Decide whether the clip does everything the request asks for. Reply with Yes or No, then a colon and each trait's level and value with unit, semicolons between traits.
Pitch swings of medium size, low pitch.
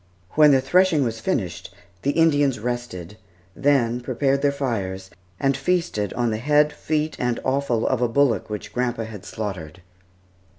Yes: average, 4.6 semitones; low, 125 Hz